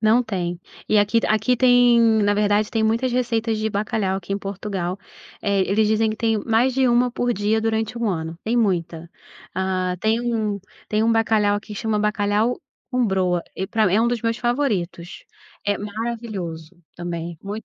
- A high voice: Yes, high, 215 Hz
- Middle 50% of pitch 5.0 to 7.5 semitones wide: No, average, 3.0 semitones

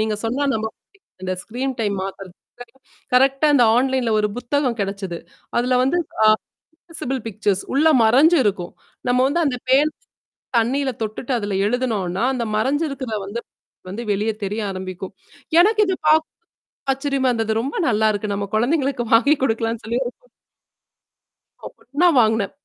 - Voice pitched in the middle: No, high, 235 Hz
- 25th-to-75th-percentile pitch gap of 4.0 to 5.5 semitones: Yes, average, 4.4 semitones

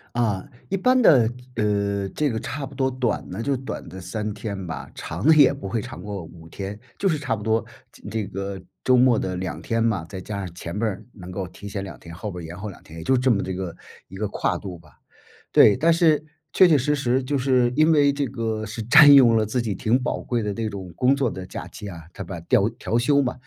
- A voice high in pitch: No, low, 110 Hz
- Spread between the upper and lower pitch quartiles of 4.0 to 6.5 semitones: Yes, average, 5.3 semitones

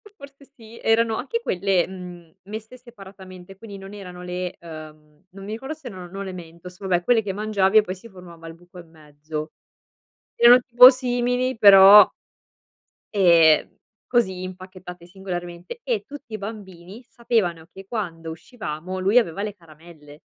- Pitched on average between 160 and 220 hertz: Yes, high, 190 Hz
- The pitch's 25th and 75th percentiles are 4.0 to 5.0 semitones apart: Yes, average, 4.3 semitones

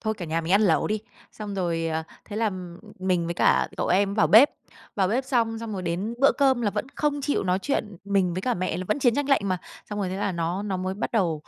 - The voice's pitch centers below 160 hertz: No, high, 200 Hz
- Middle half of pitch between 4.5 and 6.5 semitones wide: No, average, 3.8 semitones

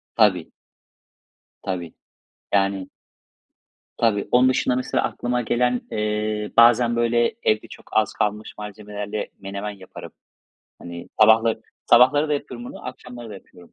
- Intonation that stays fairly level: No, average, 3.0 semitones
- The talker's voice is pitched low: Yes, low, 110 Hz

